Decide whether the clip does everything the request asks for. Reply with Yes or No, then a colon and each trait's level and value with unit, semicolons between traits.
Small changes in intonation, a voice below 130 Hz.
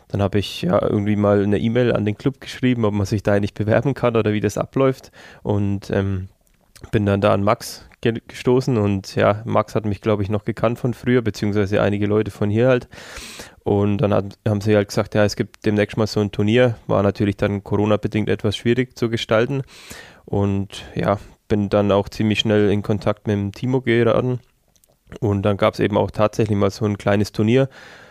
Yes: narrow, 2.1 semitones; low, 105 Hz